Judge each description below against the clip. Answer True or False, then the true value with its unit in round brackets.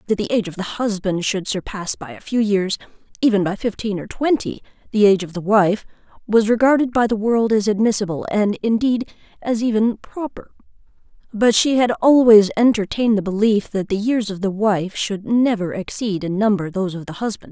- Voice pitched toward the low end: False (210 Hz)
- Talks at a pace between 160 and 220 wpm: True (185 wpm)